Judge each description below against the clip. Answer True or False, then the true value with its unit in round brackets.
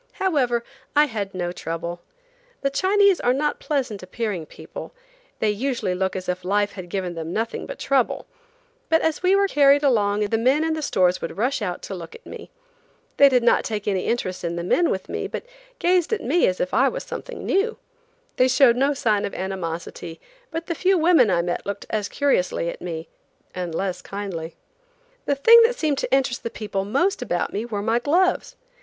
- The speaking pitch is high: True (230 Hz)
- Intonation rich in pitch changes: True (7.8 semitones)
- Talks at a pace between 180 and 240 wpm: True (200 wpm)